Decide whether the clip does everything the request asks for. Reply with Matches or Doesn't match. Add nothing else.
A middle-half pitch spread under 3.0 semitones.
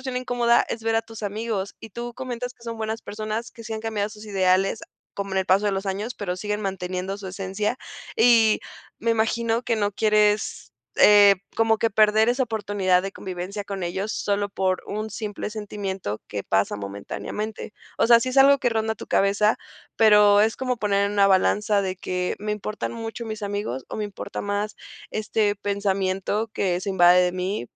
Matches